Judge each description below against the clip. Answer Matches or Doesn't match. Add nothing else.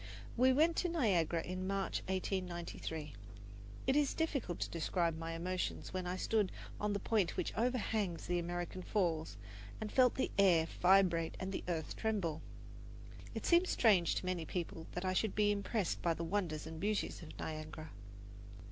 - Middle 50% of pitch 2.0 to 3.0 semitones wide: Doesn't match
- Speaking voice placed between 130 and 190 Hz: Matches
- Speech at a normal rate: Matches